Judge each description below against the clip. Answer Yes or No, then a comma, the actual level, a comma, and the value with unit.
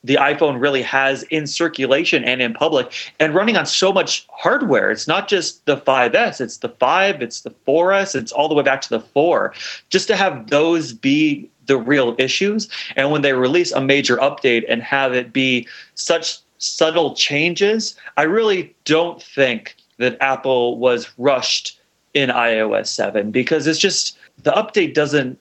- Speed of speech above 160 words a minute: Yes, average, 170 wpm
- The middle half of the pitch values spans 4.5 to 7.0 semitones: Yes, average, 5.2 semitones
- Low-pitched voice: No, medium, 145 Hz